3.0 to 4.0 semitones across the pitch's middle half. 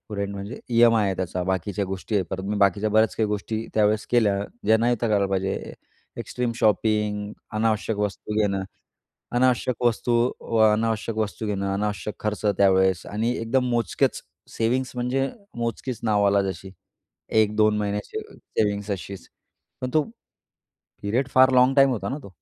No: narrow, 2.6 semitones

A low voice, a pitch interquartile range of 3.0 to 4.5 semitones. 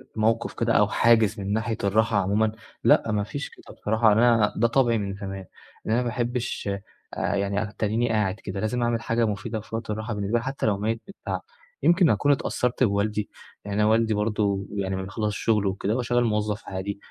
No: low, 110 Hz; narrow, 2.4 semitones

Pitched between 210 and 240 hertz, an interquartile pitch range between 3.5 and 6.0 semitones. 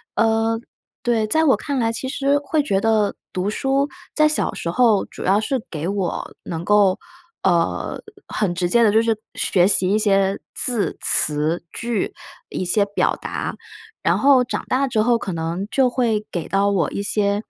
Yes: high, 215 Hz; average, 4.2 semitones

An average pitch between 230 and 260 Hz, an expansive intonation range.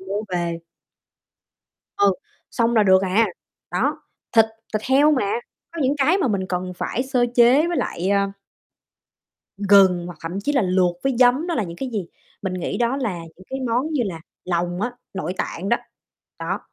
No: high, 205 Hz; wide, 5.7 semitones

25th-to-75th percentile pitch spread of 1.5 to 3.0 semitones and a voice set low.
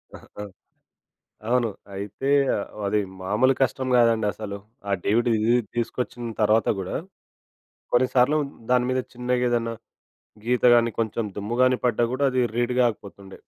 Yes: average, 2.7 semitones; low, 120 Hz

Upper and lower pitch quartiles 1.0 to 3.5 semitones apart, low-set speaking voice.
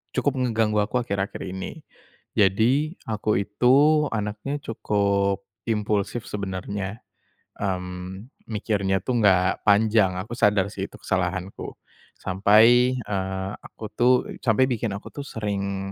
Yes: average, 3.1 semitones; low, 105 Hz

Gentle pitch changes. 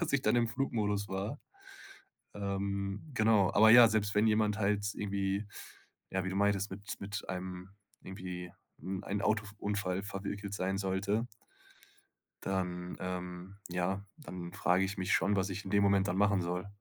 Yes: narrow, 1.6 semitones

